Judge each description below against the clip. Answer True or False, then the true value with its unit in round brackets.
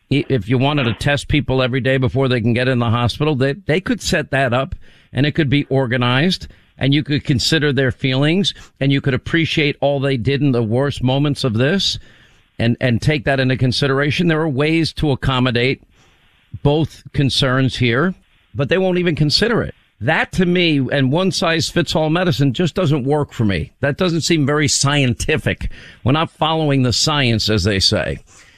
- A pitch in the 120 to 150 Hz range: True (140 Hz)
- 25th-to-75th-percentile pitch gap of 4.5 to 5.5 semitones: False (3.2 semitones)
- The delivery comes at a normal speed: True (195 wpm)